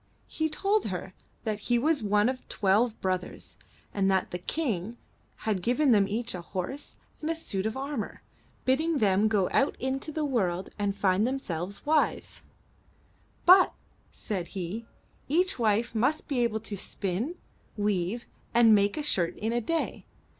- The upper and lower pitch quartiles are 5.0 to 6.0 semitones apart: Yes, wide, 5.5 semitones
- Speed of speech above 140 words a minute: Yes, average, 160 wpm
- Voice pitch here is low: No, high, 220 Hz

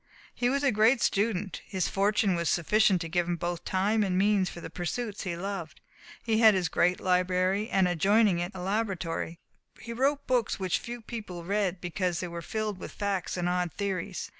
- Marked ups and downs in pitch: No, average, 3.3 semitones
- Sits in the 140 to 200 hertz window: Yes, high, 190 Hz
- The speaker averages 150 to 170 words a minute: No, average, 195 wpm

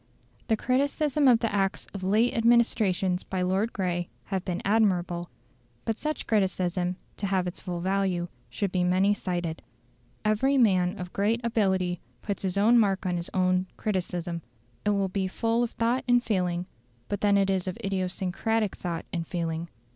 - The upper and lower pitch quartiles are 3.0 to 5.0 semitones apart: Yes, average, 3.3 semitones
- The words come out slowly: No, average, 170 wpm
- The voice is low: No, high, 190 Hz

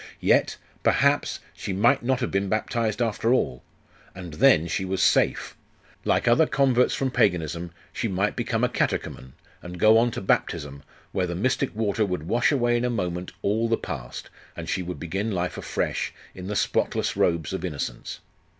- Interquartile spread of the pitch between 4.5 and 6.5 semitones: Yes, average, 5.1 semitones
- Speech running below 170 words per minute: No, average, 175 wpm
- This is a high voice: No, low, 100 Hz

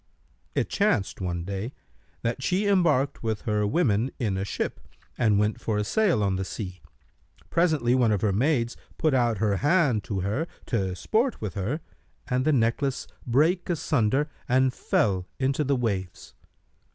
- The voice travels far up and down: Yes, wide, 5.9 semitones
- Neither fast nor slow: Yes, average, 165 wpm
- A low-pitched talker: Yes, low, 120 Hz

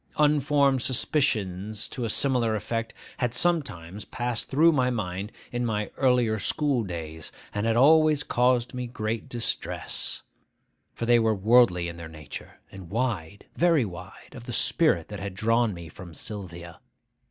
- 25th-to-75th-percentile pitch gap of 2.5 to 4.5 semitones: No, average, 4.9 semitones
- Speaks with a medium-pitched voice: No, low, 115 Hz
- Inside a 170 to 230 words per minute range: No, average, 155 wpm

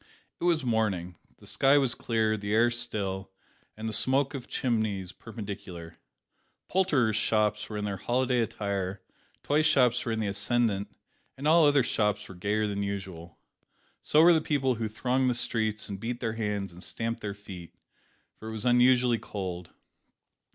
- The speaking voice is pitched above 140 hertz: No, low, 110 Hz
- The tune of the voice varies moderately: Yes, average, 3.6 semitones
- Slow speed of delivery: No, average, 170 wpm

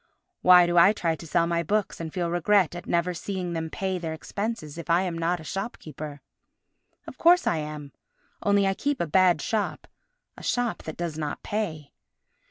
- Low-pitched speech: No, medium, 175 Hz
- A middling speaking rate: Yes, average, 185 wpm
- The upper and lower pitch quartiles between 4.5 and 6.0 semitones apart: No, average, 3.5 semitones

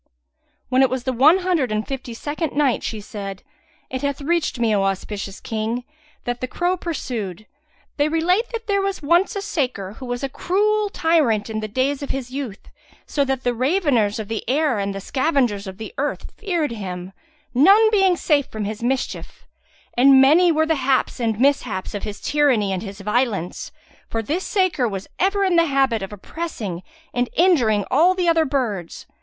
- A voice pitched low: No, very high, 260 Hz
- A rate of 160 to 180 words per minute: No, average, 190 wpm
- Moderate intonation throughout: No, wide, 7.0 semitones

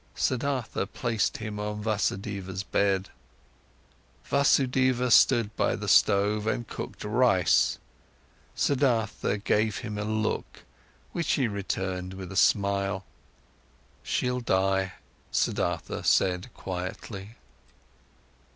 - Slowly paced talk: Yes, slow, 95 wpm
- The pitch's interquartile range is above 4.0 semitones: No, average, 3.5 semitones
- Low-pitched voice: Yes, low, 105 Hz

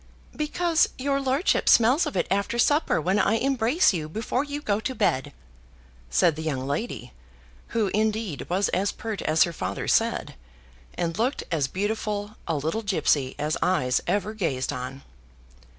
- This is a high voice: Yes, high, 205 Hz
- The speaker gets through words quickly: No, average, 160 wpm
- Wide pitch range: Yes, wide, 7.0 semitones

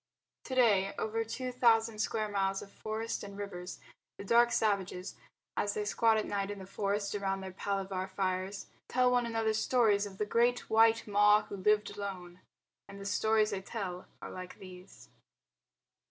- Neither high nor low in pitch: No, high, 205 Hz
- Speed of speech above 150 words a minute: Yes, average, 170 wpm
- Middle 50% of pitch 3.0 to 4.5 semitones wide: No, narrow, 2.5 semitones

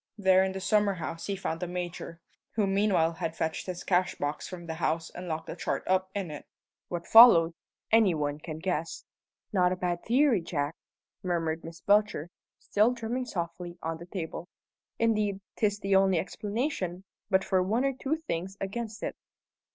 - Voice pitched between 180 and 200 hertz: Yes, medium, 185 Hz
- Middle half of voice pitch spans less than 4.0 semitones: Yes, average, 3.6 semitones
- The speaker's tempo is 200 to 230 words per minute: No, average, 175 wpm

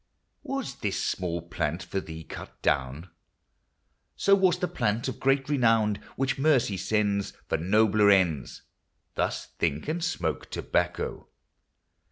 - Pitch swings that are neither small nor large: No, wide, 7.5 semitones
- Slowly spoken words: Yes, slow, 130 wpm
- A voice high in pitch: No, low, 105 Hz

